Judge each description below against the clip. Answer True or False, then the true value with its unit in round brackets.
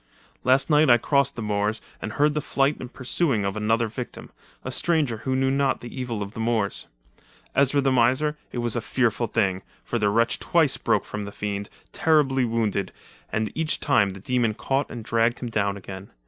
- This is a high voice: False (120 Hz)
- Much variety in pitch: False (4.2 semitones)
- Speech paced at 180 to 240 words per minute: True (200 wpm)